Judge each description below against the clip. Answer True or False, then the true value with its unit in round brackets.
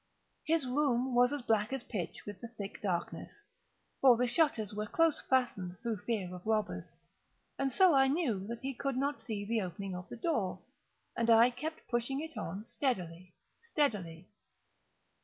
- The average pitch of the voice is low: False (235 Hz)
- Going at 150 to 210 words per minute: True (170 wpm)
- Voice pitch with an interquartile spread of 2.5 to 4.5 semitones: False (5.0 semitones)